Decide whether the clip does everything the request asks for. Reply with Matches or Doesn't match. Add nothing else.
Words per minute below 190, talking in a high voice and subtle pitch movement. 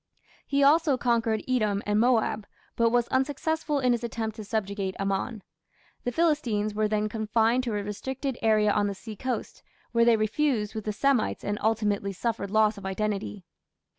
Doesn't match